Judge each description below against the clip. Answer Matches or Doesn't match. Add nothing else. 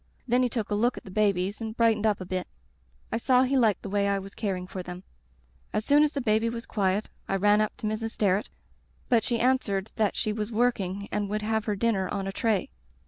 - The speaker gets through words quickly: Matches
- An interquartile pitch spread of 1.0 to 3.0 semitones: Matches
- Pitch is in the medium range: Doesn't match